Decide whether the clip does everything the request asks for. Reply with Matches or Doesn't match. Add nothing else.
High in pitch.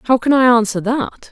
Matches